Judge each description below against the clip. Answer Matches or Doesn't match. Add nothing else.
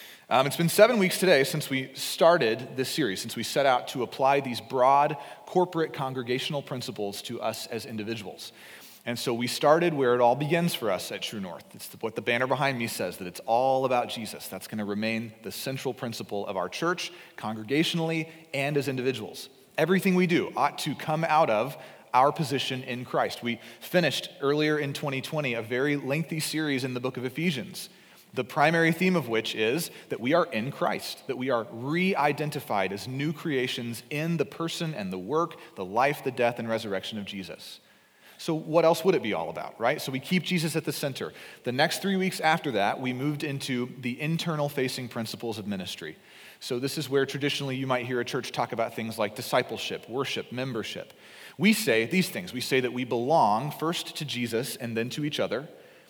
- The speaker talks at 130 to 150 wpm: Doesn't match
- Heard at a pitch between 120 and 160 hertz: Matches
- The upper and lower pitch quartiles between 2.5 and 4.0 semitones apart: Doesn't match